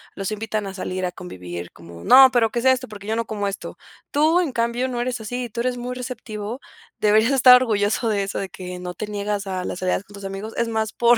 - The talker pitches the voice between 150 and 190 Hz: No, high, 215 Hz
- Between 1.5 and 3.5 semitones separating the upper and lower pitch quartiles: No, average, 3.9 semitones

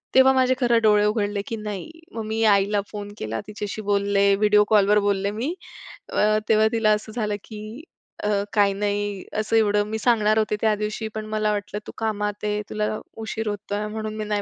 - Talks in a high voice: Yes, high, 210 Hz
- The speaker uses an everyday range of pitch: No, narrow, 1.1 semitones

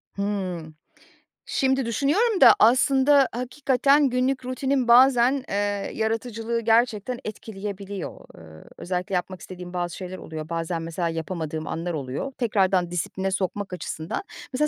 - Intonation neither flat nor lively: No, wide, 6.2 semitones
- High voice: Yes, high, 205 Hz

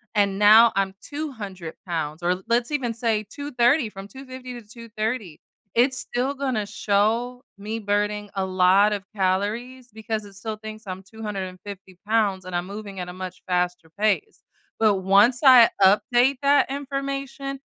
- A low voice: No, high, 215 Hz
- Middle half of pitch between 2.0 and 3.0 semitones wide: No, average, 4.3 semitones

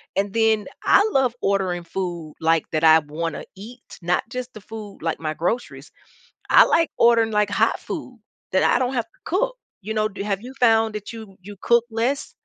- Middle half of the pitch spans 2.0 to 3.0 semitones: No, average, 4.5 semitones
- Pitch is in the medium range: No, high, 215 Hz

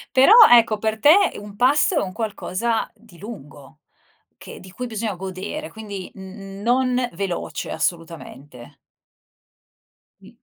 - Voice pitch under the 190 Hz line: No, high, 205 Hz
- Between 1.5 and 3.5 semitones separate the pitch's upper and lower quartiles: No, average, 4.1 semitones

